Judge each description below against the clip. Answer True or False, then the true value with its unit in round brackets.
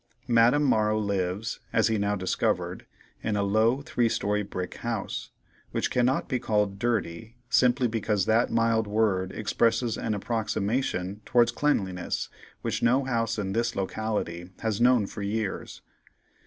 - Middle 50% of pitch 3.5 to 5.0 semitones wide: False (2.7 semitones)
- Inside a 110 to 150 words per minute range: True (140 wpm)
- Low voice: True (110 Hz)